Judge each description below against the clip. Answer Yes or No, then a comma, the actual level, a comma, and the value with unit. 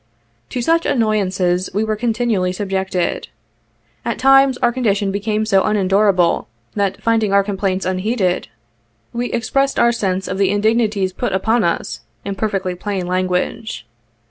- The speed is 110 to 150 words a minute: Yes, average, 145 wpm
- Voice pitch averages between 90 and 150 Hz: No, high, 200 Hz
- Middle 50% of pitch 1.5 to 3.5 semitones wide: Yes, average, 3.2 semitones